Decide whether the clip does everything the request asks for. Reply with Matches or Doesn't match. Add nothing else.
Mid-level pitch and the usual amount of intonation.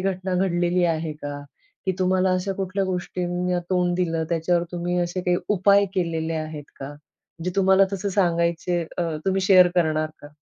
Doesn't match